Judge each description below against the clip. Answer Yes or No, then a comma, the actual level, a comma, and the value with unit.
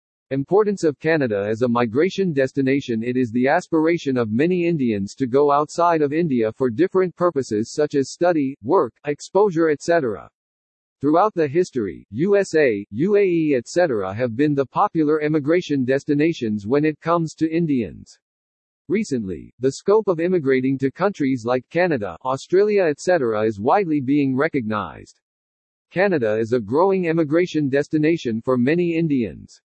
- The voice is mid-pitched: Yes, medium, 145 Hz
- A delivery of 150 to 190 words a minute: No, average, 140 wpm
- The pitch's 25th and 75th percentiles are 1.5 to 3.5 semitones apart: No, average, 5.3 semitones